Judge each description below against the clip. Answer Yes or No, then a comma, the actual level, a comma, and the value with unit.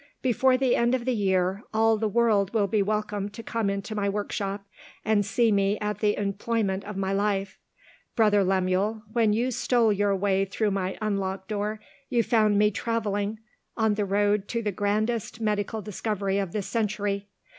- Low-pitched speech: No, high, 205 Hz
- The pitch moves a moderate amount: No, narrow, 1.8 semitones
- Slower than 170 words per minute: No, average, 175 wpm